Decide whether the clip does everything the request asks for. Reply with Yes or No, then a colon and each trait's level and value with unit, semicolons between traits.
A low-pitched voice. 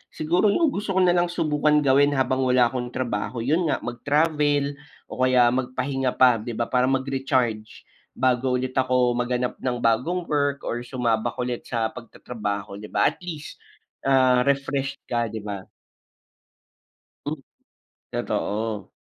Yes: low, 130 Hz